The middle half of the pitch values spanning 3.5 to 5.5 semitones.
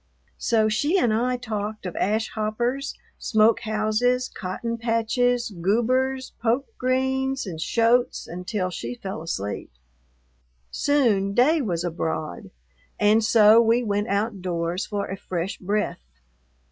Yes: average, 4.1 semitones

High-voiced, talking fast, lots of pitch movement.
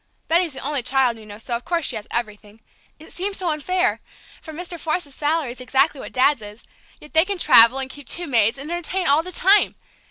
Yes: very high, 290 Hz; fast, 225 wpm; wide, 5.9 semitones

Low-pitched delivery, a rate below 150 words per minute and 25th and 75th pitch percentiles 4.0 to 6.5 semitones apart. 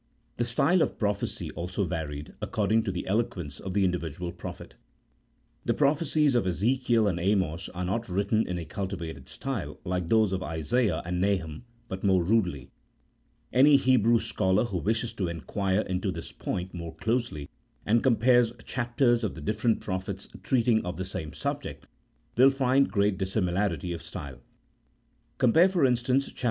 No: low, 100 Hz; average, 160 wpm; average, 5.1 semitones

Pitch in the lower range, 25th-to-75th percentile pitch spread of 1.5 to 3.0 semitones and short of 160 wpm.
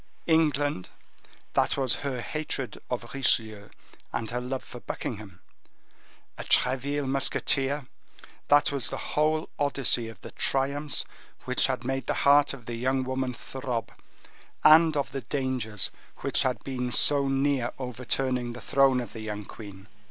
Yes: low, 130 Hz; average, 2.7 semitones; average, 145 wpm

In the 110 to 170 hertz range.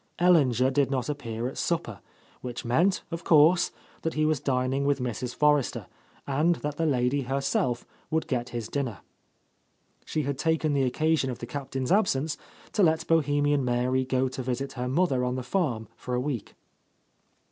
Yes: low, 135 Hz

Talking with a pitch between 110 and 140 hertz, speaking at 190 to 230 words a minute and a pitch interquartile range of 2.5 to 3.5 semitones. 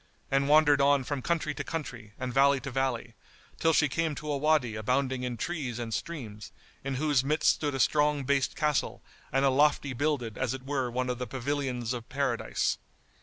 Yes: low, 135 Hz; average, 195 wpm; average, 2.8 semitones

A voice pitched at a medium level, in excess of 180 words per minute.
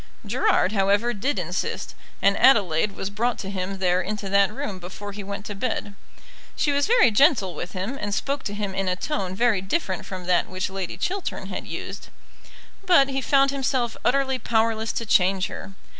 No: high, 205 Hz; average, 190 wpm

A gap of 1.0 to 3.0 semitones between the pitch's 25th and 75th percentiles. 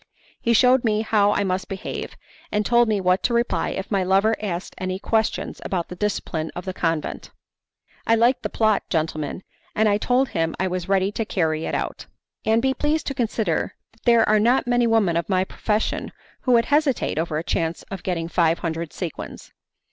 No: average, 4.4 semitones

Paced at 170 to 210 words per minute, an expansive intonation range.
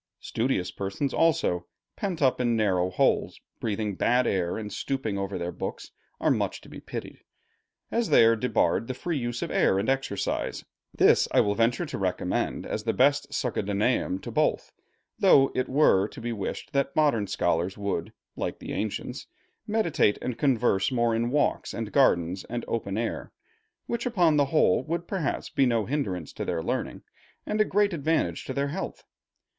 Yes: average, 175 wpm; wide, 6.1 semitones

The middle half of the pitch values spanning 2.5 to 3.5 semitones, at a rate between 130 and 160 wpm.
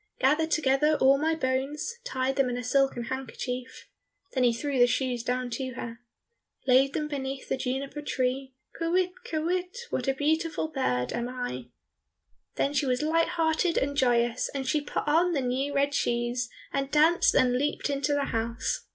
No: average, 3.1 semitones; average, 175 wpm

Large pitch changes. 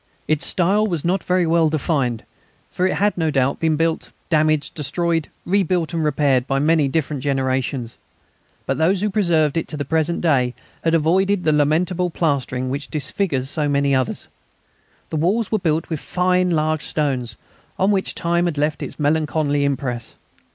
No: average, 3.4 semitones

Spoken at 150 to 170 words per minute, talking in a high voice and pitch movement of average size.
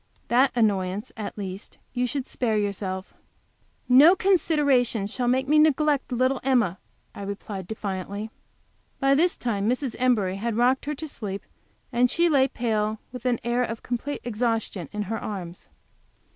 Yes: average, 160 wpm; high, 235 Hz; average, 4.4 semitones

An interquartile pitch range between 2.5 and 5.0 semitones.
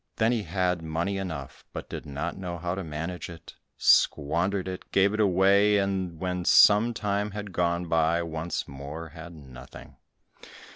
Yes: average, 3.3 semitones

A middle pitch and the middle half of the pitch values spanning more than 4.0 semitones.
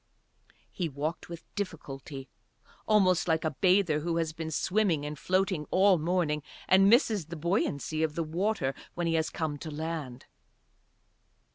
No: medium, 165 Hz; average, 3.4 semitones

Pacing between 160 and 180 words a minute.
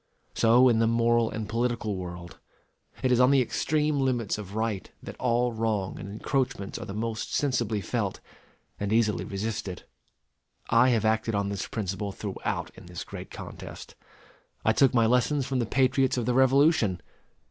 Yes: average, 170 wpm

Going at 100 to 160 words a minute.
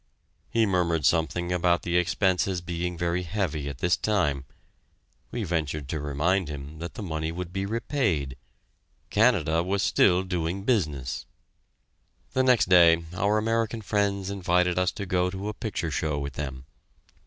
Yes: average, 155 wpm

